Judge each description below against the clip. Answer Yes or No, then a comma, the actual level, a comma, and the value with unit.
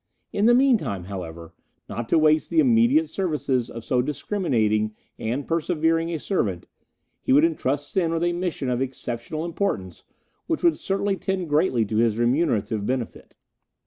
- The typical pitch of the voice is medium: Yes, medium, 150 Hz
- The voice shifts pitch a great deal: Yes, wide, 7.6 semitones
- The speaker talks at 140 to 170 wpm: Yes, average, 155 wpm